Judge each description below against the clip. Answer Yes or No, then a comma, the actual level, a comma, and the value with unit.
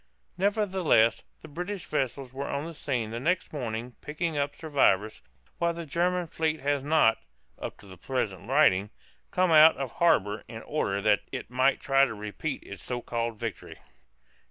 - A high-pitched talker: No, low, 135 Hz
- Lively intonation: Yes, wide, 6.2 semitones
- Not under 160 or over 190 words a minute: Yes, average, 170 wpm